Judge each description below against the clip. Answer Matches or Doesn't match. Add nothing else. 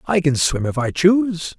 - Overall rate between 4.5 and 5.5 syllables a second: Matches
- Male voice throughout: Matches